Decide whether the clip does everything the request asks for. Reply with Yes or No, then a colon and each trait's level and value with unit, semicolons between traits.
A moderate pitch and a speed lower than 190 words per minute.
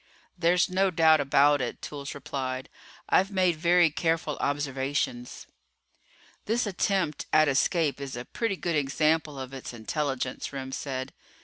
Yes: medium, 145 Hz; slow, 135 wpm